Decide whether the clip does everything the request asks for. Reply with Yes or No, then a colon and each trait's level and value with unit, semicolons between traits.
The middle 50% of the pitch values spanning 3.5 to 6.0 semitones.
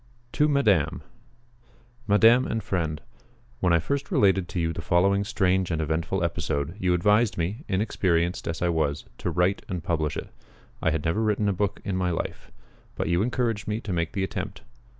Yes: average, 3.8 semitones